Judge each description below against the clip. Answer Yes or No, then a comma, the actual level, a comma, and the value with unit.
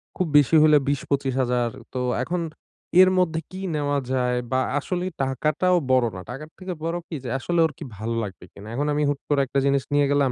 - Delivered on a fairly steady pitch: No, average, 3.8 semitones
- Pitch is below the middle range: No, medium, 145 Hz